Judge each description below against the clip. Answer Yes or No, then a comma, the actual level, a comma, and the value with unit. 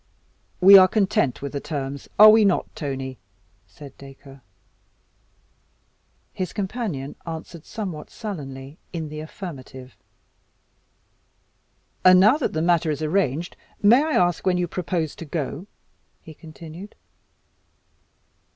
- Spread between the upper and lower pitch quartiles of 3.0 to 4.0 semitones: No, average, 5.2 semitones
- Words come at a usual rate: No, slow, 120 wpm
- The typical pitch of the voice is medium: Yes, medium, 165 Hz